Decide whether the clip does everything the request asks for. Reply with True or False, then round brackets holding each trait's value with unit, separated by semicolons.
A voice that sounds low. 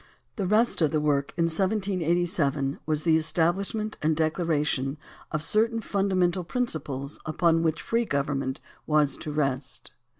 False (160 Hz)